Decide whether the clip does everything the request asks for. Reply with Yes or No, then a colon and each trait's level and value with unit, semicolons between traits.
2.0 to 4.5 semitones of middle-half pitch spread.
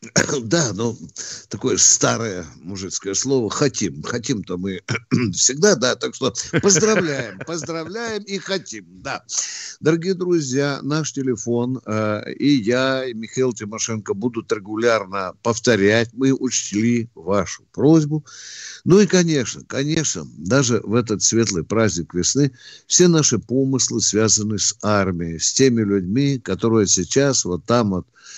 No: average, 5.2 semitones